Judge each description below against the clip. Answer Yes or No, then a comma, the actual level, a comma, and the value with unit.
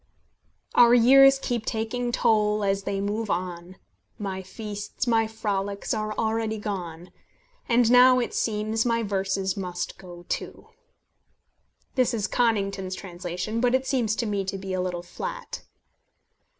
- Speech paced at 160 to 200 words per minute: No, average, 140 wpm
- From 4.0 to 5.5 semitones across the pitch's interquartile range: No, average, 3.3 semitones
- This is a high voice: Yes, high, 210 Hz